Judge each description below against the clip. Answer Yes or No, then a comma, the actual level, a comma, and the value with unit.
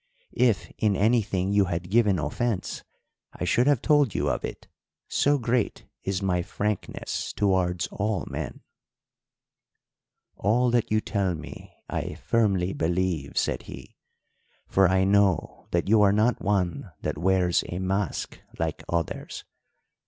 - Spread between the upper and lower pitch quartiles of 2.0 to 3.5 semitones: Yes, average, 3.2 semitones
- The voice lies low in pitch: Yes, very low, 95 Hz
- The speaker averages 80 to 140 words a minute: Yes, slow, 135 wpm